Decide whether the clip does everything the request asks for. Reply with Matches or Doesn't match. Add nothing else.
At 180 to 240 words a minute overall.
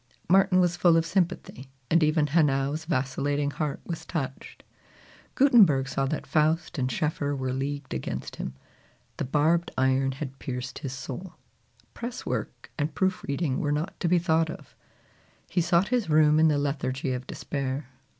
Doesn't match